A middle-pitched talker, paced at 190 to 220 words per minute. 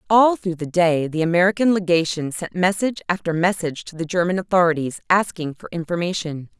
No: medium, 175 Hz; average, 165 wpm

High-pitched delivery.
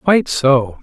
No: medium, 140 Hz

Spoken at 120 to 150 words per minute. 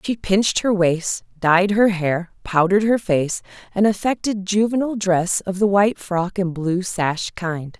No: average, 170 wpm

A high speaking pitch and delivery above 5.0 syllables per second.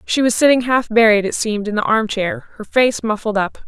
Yes: high, 225 Hz; 5.3 syllables/s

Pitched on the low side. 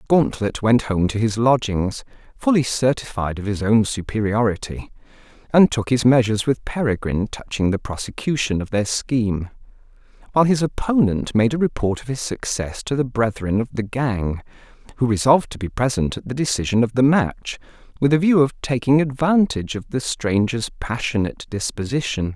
Yes: low, 120 Hz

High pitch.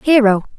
Yes: high, 240 Hz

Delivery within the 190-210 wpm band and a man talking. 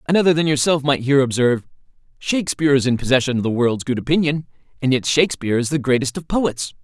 Yes: average, 200 wpm; male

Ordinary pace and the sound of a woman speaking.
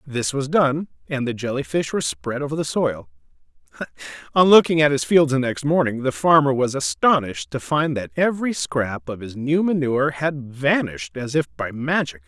No: average, 190 wpm; male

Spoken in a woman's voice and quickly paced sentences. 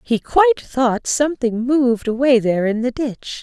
No: female; average, 175 wpm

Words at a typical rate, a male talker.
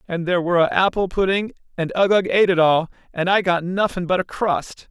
Yes: average, 195 wpm; male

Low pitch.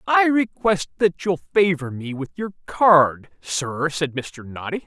No: medium, 170 Hz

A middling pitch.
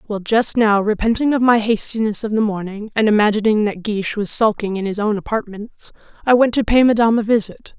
No: high, 215 Hz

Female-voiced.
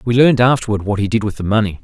No: male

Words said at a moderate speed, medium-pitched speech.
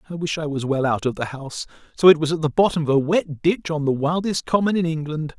No: fast, 280 wpm; medium, 155 Hz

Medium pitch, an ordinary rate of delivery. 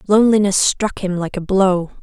No: high, 195 Hz; average, 180 wpm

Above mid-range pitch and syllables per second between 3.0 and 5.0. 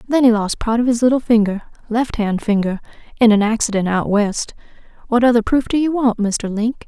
No: high, 225 Hz; 5.4 syllables/s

